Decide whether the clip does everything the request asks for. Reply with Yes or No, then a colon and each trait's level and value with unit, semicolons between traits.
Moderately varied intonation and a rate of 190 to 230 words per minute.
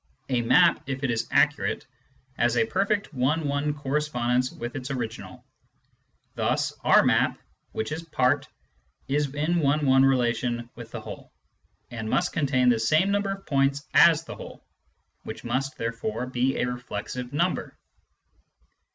No: average, 3.5 semitones; average, 150 wpm